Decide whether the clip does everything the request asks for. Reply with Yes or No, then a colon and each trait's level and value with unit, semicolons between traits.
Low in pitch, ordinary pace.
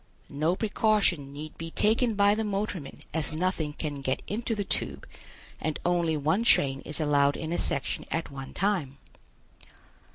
No: medium, 160 Hz; average, 160 wpm